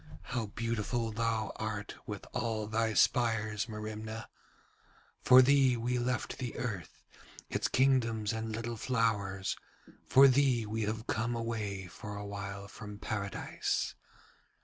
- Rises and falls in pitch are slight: Yes, narrow, 2.1 semitones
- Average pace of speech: No, slow, 125 wpm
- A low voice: Yes, low, 110 Hz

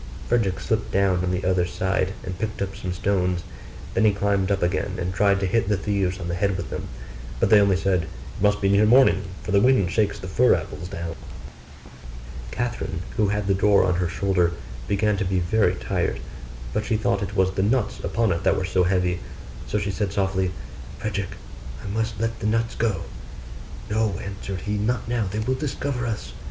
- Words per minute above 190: Yes, fast, 205 wpm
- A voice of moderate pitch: No, low, 100 Hz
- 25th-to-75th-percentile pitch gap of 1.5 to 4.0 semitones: Yes, narrow, 2.4 semitones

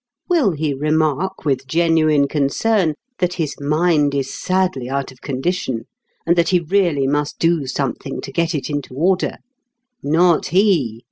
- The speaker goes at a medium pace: Yes, average, 150 wpm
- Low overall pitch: No, medium, 155 Hz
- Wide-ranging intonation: No, average, 4.1 semitones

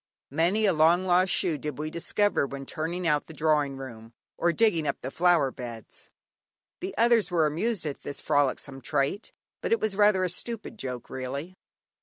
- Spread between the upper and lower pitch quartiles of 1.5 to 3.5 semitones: No, average, 5.2 semitones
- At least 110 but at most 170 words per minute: No, average, 180 wpm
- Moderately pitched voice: Yes, medium, 160 Hz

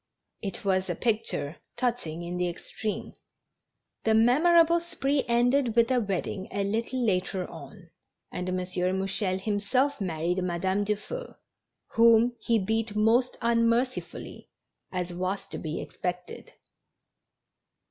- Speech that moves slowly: Yes, slow, 120 wpm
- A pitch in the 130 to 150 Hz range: No, high, 210 Hz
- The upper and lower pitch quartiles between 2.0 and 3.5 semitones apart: No, average, 4.5 semitones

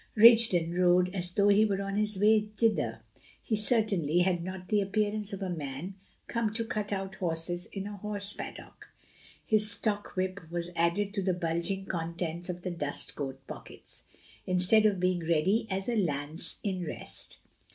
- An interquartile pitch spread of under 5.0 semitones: Yes, average, 3.1 semitones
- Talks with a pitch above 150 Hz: Yes, high, 190 Hz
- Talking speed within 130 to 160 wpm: No, average, 170 wpm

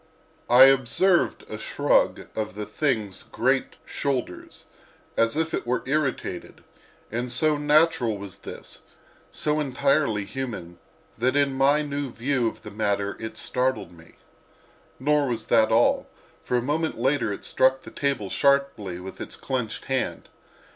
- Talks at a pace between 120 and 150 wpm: Yes, average, 140 wpm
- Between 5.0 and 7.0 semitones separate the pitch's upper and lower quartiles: No, average, 4.5 semitones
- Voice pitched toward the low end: Yes, low, 130 Hz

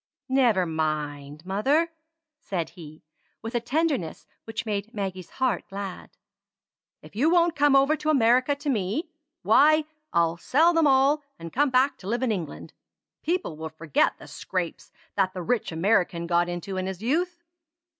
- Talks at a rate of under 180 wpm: Yes, average, 160 wpm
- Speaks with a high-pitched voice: Yes, high, 215 Hz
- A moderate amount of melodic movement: No, wide, 8.4 semitones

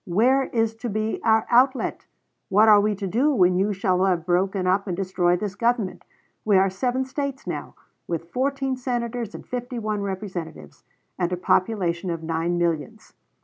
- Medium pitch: No, high, 200 Hz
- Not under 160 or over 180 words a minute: Yes, average, 175 wpm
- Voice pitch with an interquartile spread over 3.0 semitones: Yes, average, 4.6 semitones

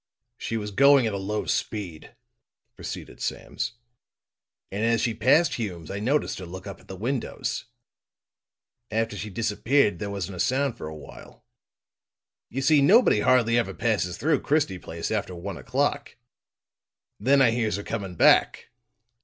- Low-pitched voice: Yes, low, 110 Hz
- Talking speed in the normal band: Yes, average, 155 wpm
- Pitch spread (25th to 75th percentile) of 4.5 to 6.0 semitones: Yes, average, 5.2 semitones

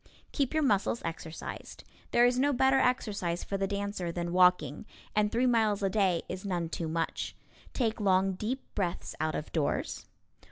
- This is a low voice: No, high, 195 Hz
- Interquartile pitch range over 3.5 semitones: Yes, average, 5.2 semitones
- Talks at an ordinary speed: Yes, average, 170 wpm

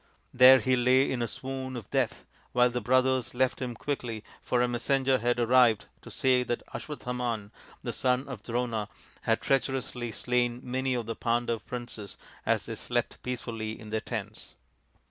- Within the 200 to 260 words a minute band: No, average, 170 wpm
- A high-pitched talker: No, low, 125 Hz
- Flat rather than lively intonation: Yes, narrow, 1.7 semitones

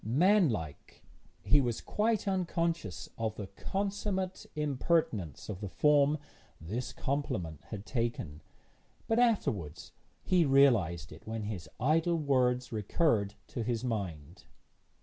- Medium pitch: No, low, 125 Hz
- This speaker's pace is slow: Yes, slow, 115 wpm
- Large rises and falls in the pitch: Yes, wide, 8.4 semitones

